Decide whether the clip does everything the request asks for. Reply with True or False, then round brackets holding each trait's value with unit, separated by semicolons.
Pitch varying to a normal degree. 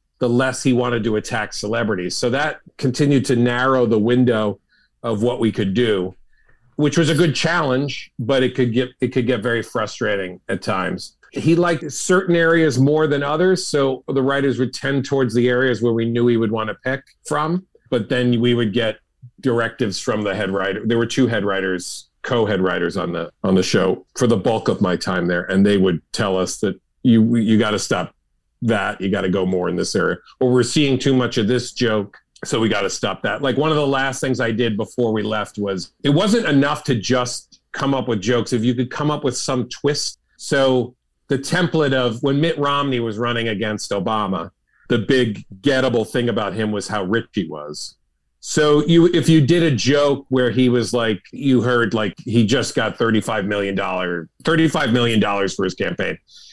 True (4.2 semitones)